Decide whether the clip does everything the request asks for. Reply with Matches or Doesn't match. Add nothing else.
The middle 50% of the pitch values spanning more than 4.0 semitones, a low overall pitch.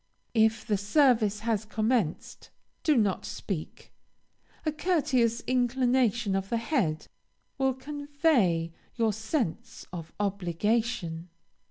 Doesn't match